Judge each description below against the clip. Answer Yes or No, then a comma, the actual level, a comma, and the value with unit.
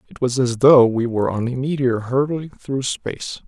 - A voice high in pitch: No, low, 130 Hz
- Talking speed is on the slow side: No, fast, 205 wpm